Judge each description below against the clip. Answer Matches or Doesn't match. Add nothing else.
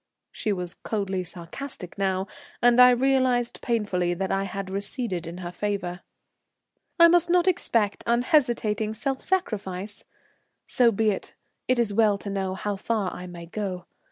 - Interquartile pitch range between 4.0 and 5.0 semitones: Matches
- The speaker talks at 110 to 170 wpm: Matches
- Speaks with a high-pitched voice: Matches